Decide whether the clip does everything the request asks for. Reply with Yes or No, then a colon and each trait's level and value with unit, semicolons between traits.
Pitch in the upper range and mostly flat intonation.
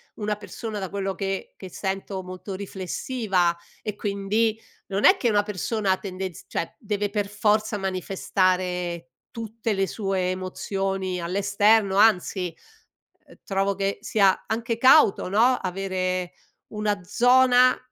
Yes: high, 195 Hz; narrow, 2.2 semitones